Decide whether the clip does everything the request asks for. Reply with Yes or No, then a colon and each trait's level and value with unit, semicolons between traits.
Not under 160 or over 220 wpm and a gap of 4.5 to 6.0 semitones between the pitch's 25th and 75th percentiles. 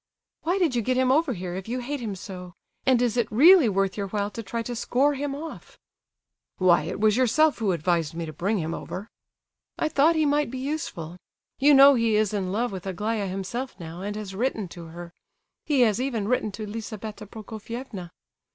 Yes: fast, 205 wpm; average, 5.2 semitones